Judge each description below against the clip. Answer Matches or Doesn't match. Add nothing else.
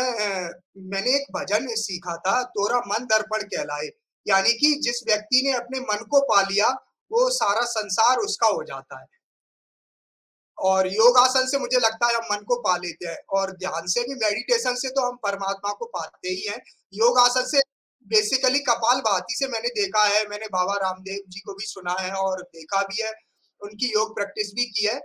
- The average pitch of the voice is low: Doesn't match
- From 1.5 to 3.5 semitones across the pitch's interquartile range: Doesn't match